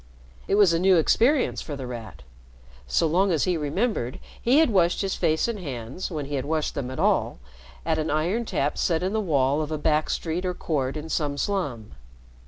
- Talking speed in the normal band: No, fast, 210 wpm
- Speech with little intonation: No, average, 4.8 semitones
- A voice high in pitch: No, medium, 160 Hz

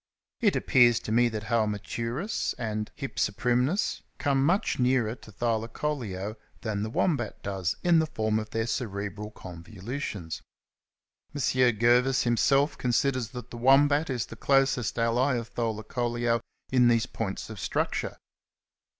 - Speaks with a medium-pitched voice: No, low, 120 Hz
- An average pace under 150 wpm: Yes, slow, 135 wpm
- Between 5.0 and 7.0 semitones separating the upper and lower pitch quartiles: No, average, 3.3 semitones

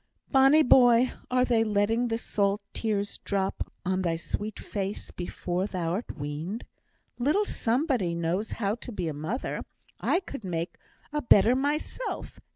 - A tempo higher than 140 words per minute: Yes, average, 150 wpm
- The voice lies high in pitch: Yes, high, 210 Hz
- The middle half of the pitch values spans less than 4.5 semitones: No, average, 5.2 semitones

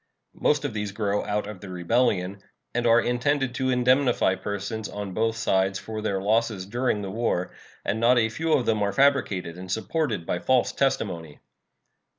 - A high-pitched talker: No, low, 110 Hz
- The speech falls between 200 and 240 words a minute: No, average, 175 wpm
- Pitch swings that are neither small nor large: Yes, average, 4.0 semitones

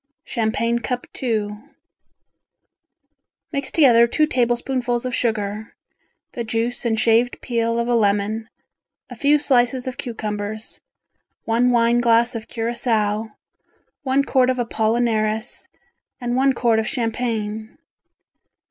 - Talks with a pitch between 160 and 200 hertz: No, high, 235 Hz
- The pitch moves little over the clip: Yes, narrow, 2.0 semitones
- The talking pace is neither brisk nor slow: No, slow, 115 wpm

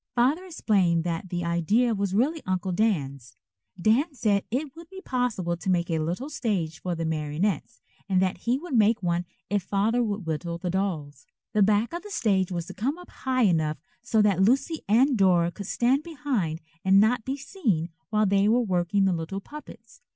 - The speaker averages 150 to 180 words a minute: No, average, 195 wpm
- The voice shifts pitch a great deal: Yes, wide, 6.1 semitones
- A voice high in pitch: Yes, high, 200 Hz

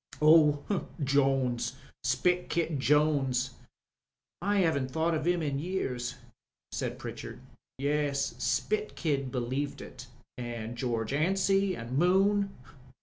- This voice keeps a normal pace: No, slow, 110 wpm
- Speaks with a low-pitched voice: No, medium, 145 Hz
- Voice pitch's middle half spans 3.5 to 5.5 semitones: Yes, average, 5.1 semitones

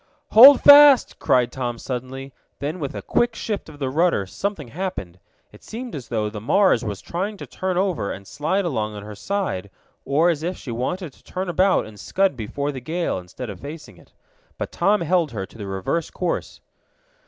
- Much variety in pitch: Yes, wide, 8.6 semitones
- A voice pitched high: No, medium, 145 Hz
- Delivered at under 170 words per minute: No, average, 200 wpm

